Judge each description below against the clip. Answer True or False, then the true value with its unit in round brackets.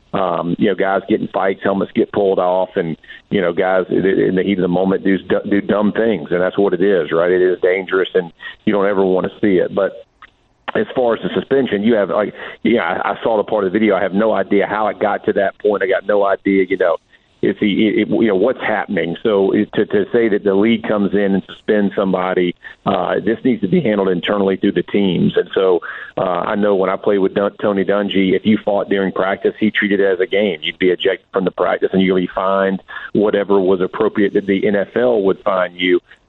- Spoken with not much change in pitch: True (1.7 semitones)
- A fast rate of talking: True (235 wpm)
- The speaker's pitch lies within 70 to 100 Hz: True (95 Hz)